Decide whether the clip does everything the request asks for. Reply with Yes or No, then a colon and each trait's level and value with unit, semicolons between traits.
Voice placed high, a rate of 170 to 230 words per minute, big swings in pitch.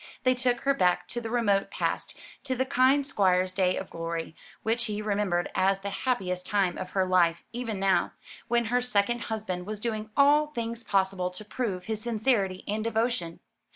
No: high, 215 Hz; average, 185 wpm; average, 4.3 semitones